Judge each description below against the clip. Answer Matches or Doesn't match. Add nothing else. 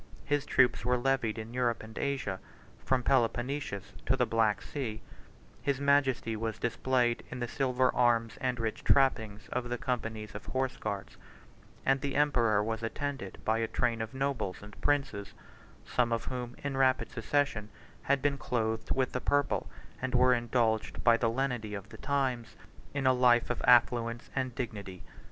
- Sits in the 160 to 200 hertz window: Doesn't match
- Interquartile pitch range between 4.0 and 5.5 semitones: Doesn't match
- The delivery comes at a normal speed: Matches